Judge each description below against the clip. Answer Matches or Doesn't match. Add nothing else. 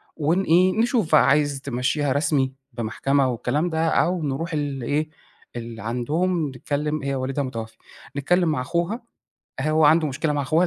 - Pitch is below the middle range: Doesn't match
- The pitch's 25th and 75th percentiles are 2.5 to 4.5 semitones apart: Matches